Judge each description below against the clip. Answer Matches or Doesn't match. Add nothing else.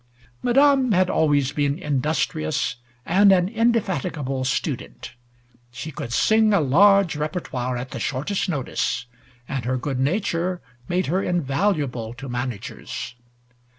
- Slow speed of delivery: Matches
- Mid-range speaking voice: Matches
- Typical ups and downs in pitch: Doesn't match